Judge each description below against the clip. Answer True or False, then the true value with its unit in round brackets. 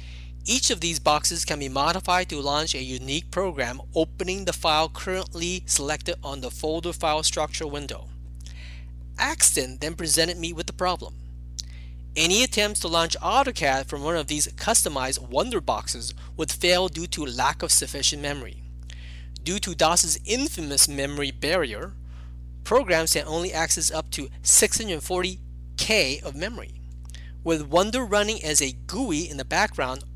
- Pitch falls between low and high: True (150 Hz)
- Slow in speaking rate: False (150 wpm)